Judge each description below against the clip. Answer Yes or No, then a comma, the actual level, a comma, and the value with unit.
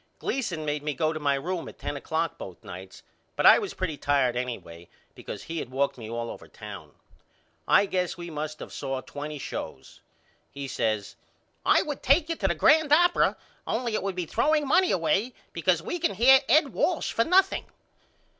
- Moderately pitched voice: Yes, medium, 165 Hz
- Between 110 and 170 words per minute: No, average, 190 wpm